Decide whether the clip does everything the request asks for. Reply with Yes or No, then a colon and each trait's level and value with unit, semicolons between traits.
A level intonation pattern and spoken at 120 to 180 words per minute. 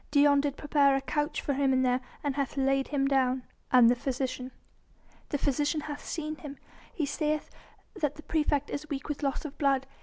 No: narrow, 1.7 semitones; average, 190 wpm